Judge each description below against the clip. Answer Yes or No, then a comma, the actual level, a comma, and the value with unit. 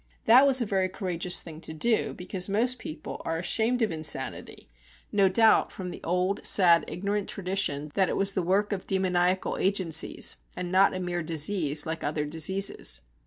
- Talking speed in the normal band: Yes, average, 175 wpm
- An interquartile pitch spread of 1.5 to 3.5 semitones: Yes, average, 3.2 semitones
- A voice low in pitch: No, medium, 185 Hz